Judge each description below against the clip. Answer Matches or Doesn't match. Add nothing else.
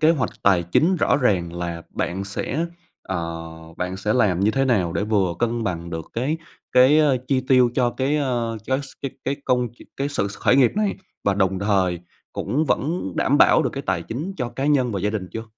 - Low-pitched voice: Matches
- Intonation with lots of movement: Matches